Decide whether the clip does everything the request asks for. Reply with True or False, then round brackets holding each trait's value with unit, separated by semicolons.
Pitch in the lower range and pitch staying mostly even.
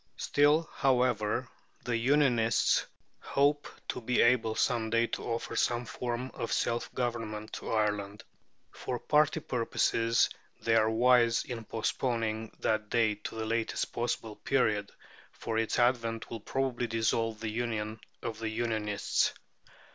True (115 Hz; 1.8 semitones)